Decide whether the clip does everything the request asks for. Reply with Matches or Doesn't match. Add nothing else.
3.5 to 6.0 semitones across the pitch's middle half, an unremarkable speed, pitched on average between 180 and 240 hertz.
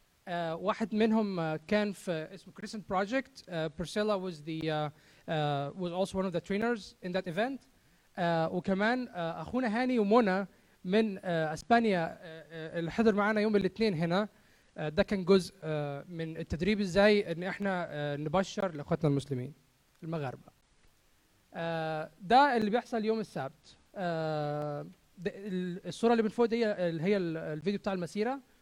Doesn't match